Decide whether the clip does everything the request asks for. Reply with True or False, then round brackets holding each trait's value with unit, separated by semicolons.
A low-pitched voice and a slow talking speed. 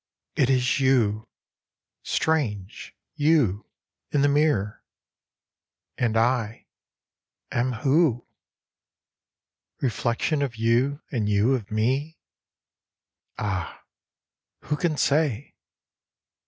True (125 Hz; 85 wpm)